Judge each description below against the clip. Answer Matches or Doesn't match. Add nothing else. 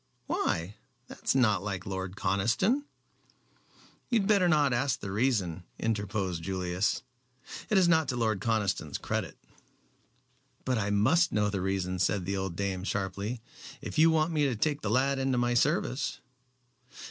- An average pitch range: Doesn't match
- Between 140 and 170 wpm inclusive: Matches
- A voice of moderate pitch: Doesn't match